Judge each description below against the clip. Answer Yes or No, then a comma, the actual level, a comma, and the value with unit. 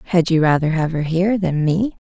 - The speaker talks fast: Yes, fast, 230 wpm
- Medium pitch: Yes, medium, 170 Hz